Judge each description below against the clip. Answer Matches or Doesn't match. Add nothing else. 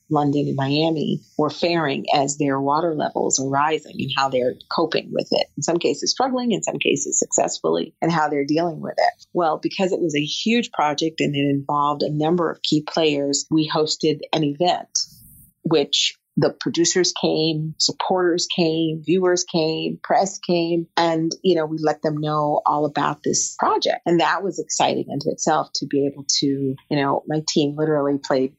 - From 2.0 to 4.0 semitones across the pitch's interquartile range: Matches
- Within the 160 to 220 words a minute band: Matches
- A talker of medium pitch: Matches